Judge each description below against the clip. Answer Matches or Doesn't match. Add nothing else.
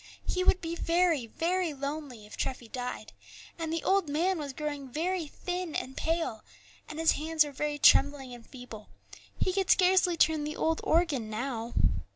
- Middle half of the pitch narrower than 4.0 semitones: Doesn't match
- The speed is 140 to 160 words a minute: Doesn't match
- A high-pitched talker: Matches